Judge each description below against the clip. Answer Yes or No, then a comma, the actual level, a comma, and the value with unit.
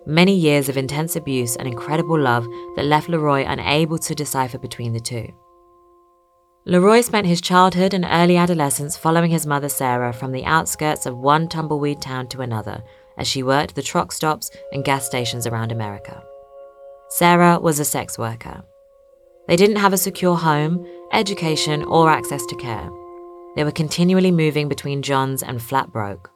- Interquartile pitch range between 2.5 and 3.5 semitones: No, average, 4.9 semitones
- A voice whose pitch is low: No, medium, 150 Hz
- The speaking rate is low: No, average, 165 wpm